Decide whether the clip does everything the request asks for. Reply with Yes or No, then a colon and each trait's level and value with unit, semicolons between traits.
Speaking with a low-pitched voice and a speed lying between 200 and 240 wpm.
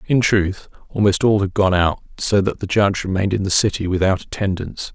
Yes: very low, 95 Hz; fast, 205 wpm